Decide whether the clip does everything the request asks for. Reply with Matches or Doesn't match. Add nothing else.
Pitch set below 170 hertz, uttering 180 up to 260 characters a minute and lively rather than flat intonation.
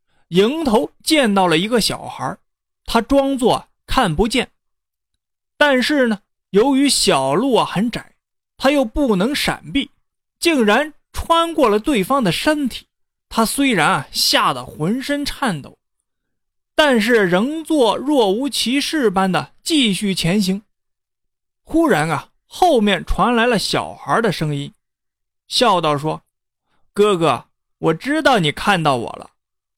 Doesn't match